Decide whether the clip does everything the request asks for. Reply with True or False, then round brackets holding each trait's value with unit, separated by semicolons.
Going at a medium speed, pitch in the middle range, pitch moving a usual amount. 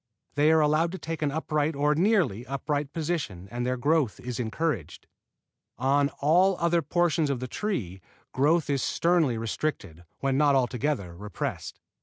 True (155 wpm; 145 Hz; 4.5 semitones)